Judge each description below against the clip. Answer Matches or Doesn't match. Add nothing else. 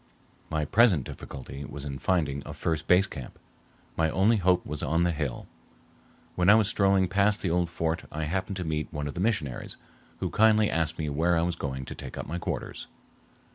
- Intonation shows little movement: Doesn't match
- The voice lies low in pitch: Matches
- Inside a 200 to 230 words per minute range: Matches